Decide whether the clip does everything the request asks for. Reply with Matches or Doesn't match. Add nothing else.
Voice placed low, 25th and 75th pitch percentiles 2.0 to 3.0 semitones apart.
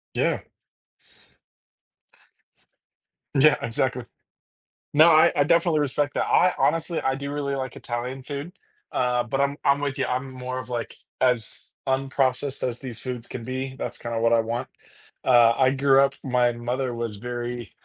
Matches